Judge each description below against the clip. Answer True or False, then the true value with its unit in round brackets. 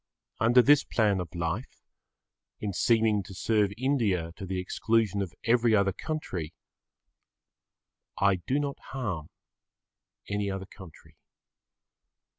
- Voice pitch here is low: True (100 Hz)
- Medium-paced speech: False (115 wpm)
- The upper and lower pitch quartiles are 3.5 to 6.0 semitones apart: True (3.9 semitones)